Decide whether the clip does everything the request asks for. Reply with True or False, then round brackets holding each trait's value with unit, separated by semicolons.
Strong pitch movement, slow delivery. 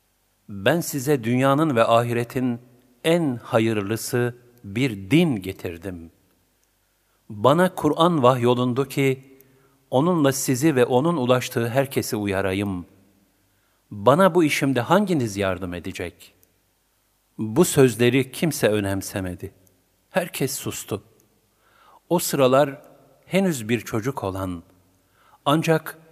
True (5.9 semitones; 90 wpm)